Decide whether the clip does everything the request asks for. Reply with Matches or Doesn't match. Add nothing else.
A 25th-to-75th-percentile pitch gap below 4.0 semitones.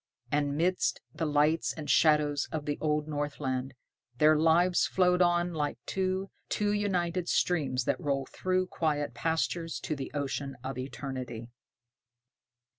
Matches